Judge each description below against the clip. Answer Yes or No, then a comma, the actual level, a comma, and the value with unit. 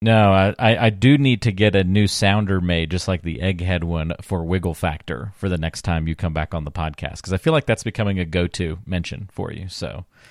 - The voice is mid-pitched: No, very low, 95 Hz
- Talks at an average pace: No, fast, 245 wpm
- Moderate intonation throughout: Yes, average, 3.6 semitones